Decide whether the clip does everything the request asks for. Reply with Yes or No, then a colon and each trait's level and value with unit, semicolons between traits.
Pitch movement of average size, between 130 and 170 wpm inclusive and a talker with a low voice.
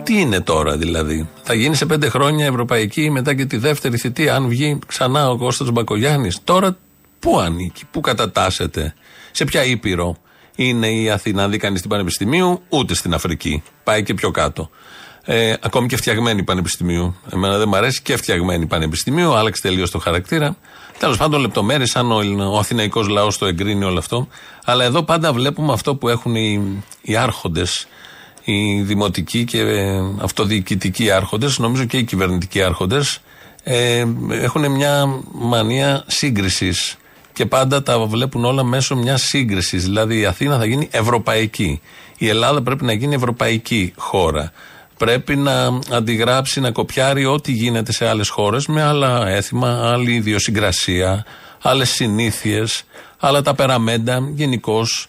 Yes: average, 4.7 semitones; average, 150 wpm; low, 115 Hz